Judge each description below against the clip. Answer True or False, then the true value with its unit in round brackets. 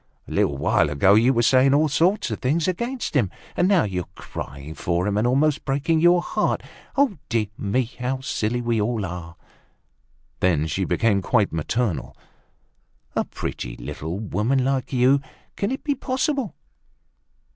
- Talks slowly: False (155 wpm)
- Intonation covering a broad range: True (7.2 semitones)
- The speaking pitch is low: True (120 Hz)